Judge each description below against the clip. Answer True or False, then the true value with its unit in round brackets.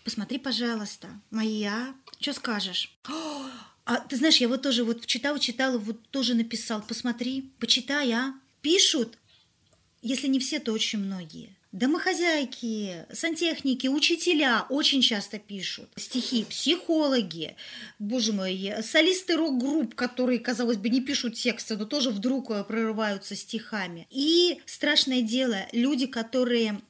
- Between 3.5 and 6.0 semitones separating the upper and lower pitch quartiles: True (3.9 semitones)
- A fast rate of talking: False (125 wpm)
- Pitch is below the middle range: False (245 Hz)